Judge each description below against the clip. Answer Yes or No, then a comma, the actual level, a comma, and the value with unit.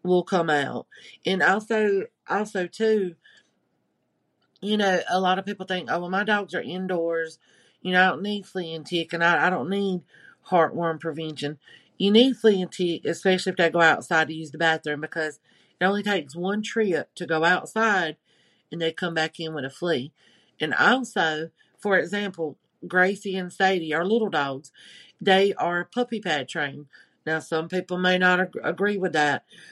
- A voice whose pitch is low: No, medium, 180 Hz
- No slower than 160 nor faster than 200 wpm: Yes, average, 180 wpm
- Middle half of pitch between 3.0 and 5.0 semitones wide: Yes, average, 3.4 semitones